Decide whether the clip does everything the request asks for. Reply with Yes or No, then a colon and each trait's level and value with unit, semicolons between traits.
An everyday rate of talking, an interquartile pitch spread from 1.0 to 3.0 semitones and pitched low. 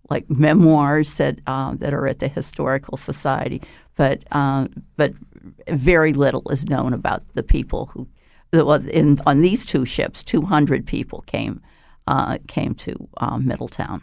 No: average, 150 wpm; narrow, 2.5 semitones; medium, 145 Hz